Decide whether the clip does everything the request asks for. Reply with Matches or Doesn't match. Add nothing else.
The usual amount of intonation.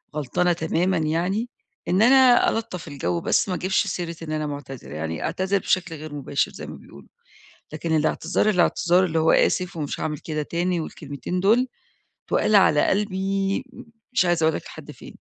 Matches